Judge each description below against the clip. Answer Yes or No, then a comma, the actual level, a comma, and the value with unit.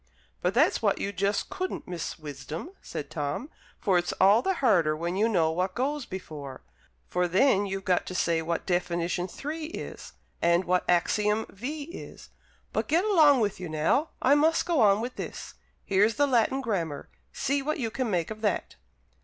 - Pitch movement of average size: No, wide, 7.5 semitones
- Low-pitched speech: No, high, 200 Hz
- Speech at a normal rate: Yes, average, 185 wpm